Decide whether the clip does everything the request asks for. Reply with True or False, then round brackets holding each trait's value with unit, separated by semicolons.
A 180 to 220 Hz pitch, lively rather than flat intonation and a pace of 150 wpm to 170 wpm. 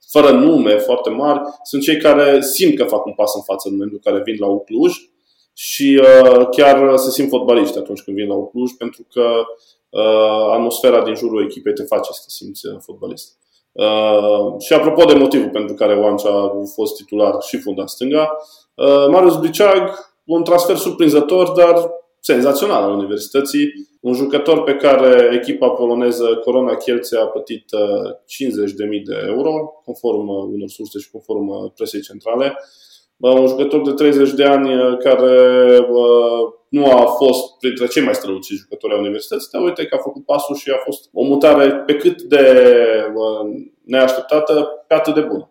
False (140 Hz; 5.7 semitones; 165 wpm)